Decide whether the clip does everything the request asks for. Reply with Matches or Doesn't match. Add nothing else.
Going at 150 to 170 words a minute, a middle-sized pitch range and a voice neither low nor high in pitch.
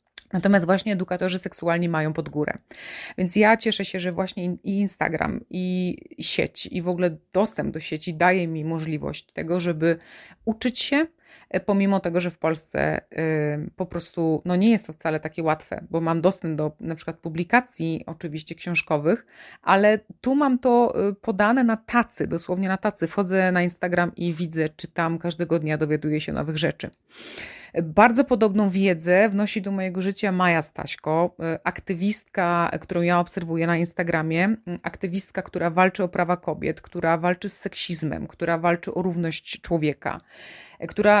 Matches